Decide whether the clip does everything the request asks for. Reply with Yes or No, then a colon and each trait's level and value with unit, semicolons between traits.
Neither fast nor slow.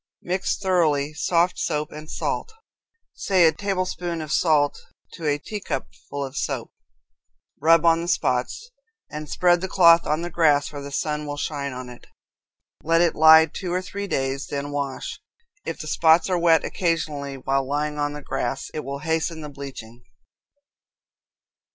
Yes: average, 165 wpm